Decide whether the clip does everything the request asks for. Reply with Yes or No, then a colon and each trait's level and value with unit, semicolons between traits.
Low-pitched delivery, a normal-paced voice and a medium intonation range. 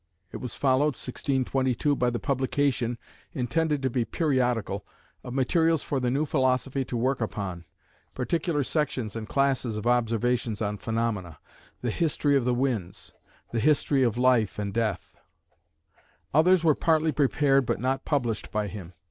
Yes: low, 130 Hz; average, 150 wpm; average, 3.6 semitones